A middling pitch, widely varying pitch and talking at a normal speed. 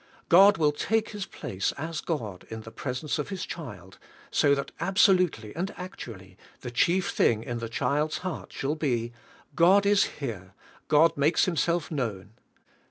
Yes: medium, 150 Hz; wide, 7.6 semitones; average, 160 wpm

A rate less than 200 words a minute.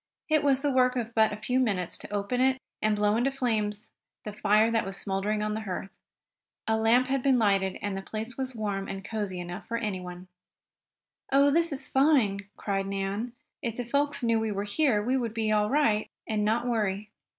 No: fast, 205 wpm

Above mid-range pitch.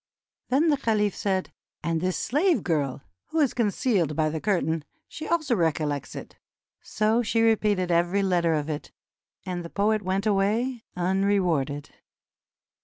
Yes: high, 195 Hz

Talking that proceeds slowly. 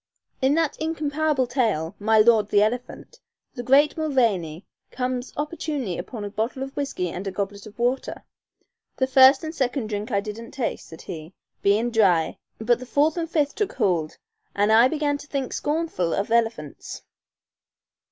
No: average, 165 wpm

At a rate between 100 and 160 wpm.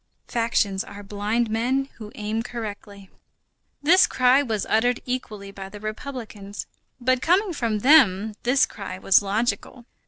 Yes: slow, 135 wpm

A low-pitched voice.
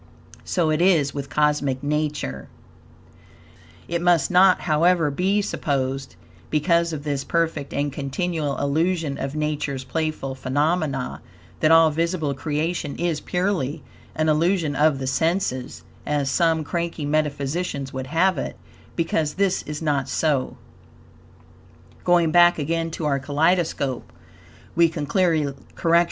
No: medium, 150 Hz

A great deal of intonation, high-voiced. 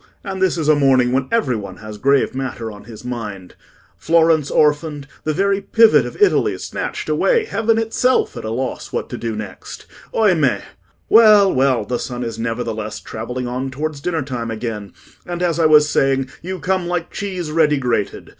No: wide, 6.8 semitones; medium, 140 Hz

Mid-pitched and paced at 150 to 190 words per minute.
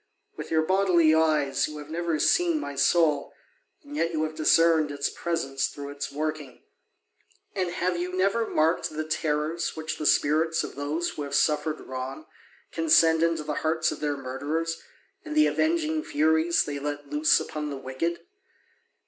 Yes: medium, 155 Hz; average, 170 wpm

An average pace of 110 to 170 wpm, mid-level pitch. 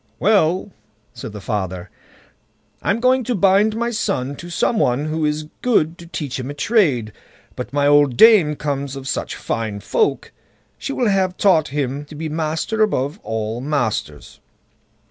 Yes: average, 165 wpm; medium, 150 Hz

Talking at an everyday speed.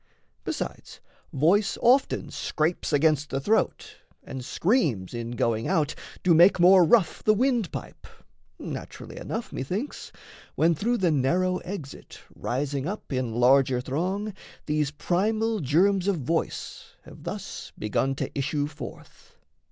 No: slow, 130 wpm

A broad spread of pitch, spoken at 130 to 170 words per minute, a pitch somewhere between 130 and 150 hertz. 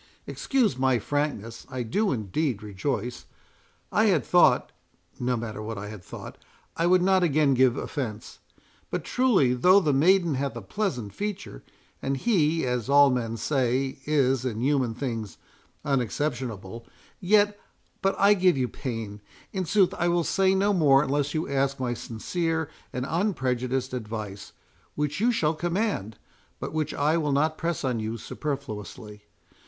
Yes: wide, 6.1 semitones; average, 145 wpm; low, 135 Hz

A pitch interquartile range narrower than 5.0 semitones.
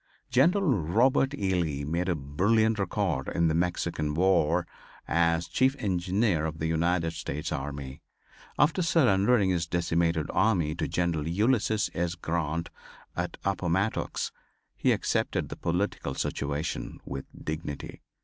Yes: average, 4.2 semitones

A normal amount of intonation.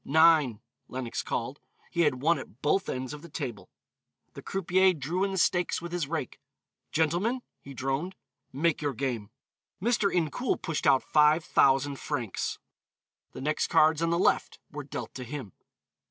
Yes: average, 4.2 semitones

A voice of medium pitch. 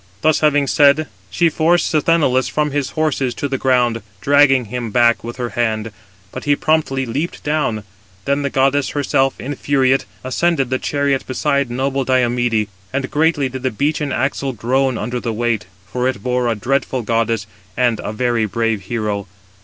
No: low, 130 Hz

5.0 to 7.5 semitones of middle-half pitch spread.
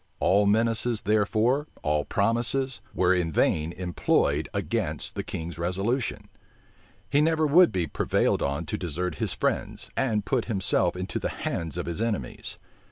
Yes: wide, 5.4 semitones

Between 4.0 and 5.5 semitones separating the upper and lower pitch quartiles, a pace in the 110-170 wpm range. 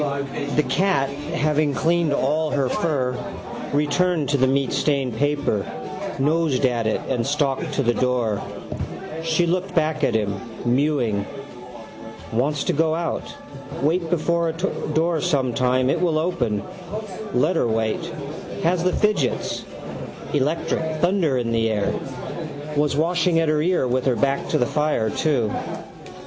Yes: average, 4.4 semitones; average, 140 wpm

